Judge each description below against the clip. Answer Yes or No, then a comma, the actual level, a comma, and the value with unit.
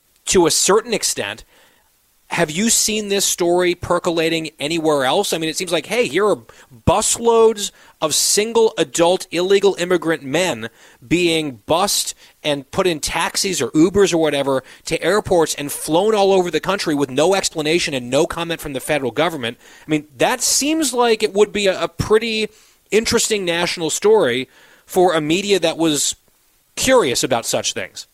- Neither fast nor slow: Yes, average, 165 wpm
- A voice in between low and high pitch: Yes, medium, 175 Hz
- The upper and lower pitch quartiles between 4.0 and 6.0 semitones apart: Yes, average, 4.9 semitones